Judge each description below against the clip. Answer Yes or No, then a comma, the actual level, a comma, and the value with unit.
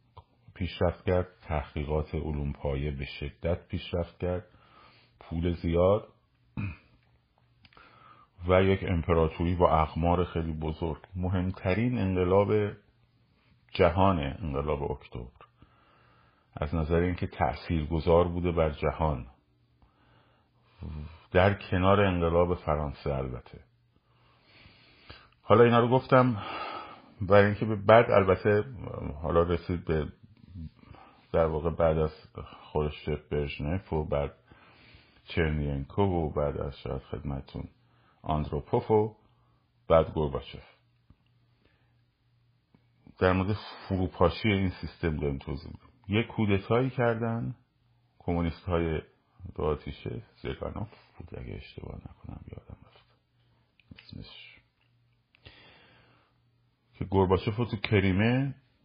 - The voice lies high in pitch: No, very low, 95 Hz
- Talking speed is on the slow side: Yes, slow, 95 wpm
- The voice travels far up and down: Yes, wide, 6.1 semitones